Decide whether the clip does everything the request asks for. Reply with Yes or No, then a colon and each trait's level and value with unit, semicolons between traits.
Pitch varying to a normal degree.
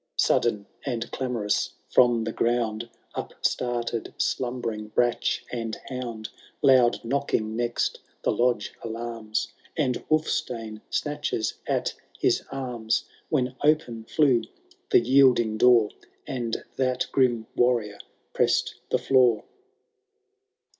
No: narrow, 2.3 semitones